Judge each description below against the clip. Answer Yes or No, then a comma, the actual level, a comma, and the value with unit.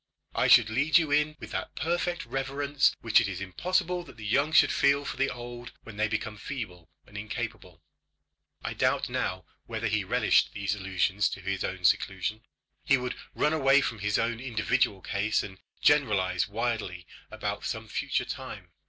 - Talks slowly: No, average, 175 wpm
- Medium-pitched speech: No, low, 115 Hz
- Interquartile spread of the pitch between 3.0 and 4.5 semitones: No, wide, 5.4 semitones